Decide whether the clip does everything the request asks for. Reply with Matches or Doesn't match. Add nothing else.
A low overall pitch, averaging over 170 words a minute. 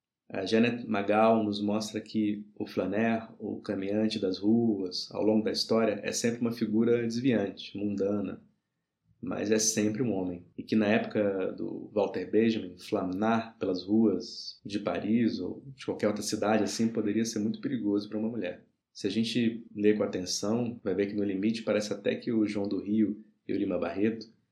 Matches